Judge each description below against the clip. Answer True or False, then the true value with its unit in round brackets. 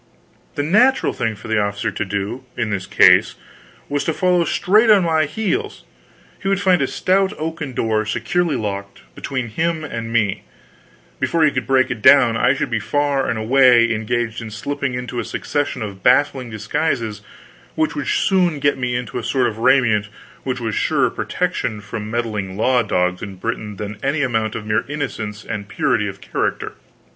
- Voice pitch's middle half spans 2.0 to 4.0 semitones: False (5.1 semitones)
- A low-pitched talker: True (120 Hz)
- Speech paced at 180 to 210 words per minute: True (185 wpm)